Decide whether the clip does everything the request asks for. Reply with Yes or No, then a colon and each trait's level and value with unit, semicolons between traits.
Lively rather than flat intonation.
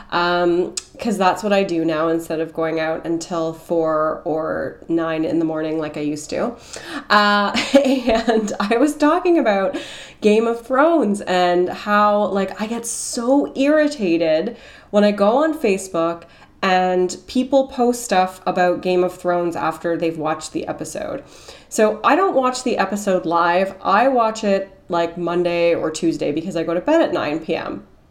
Yes: wide, 5.7 semitones